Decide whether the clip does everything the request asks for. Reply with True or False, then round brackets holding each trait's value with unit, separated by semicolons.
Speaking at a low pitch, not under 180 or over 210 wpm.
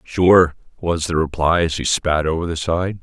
True (85 Hz; 200 wpm)